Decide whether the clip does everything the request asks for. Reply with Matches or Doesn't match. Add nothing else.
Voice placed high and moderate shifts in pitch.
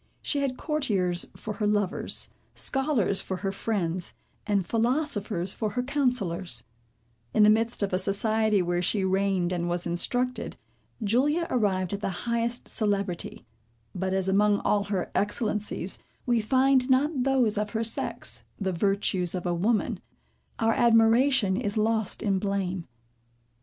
Matches